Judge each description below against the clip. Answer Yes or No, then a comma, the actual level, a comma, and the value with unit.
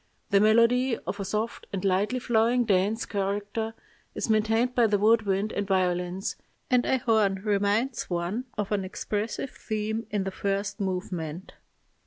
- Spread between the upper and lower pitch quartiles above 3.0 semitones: No, narrow, 2.6 semitones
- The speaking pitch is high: Yes, high, 210 Hz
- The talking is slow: No, average, 155 wpm